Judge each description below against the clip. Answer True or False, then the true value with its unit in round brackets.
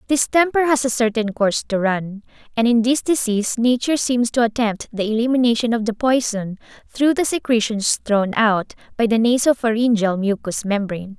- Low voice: False (230 Hz)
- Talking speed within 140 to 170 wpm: True (165 wpm)